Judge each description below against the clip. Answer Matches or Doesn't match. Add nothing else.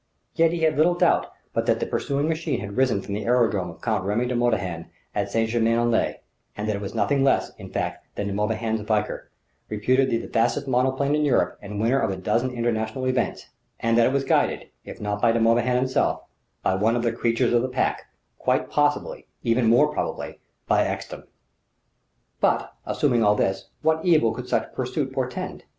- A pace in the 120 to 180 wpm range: Doesn't match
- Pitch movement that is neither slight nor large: Matches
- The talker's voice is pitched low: Matches